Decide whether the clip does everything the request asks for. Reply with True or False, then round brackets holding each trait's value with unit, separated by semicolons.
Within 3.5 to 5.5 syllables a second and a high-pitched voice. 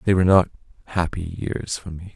False (5.4 syllables/s; 90 Hz)